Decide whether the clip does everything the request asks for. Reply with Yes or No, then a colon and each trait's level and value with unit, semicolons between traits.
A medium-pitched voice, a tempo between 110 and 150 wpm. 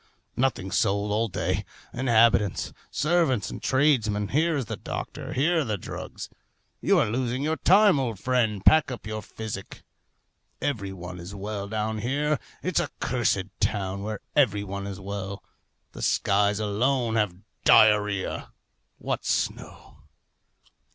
No: low, 110 Hz; average, 140 wpm